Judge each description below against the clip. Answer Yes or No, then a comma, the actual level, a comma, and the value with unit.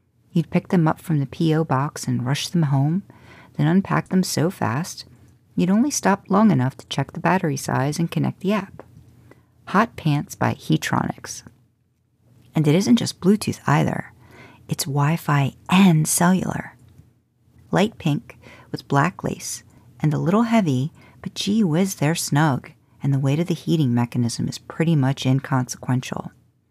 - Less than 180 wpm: Yes, average, 160 wpm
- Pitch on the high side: No, medium, 140 Hz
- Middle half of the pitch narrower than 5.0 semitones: No, wide, 5.5 semitones